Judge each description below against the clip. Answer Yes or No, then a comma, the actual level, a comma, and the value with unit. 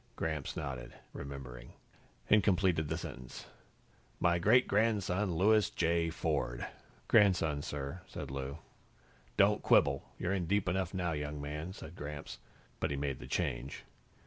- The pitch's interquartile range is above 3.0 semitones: Yes, average, 4.9 semitones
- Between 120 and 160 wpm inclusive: Yes, average, 140 wpm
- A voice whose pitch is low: Yes, very low, 80 Hz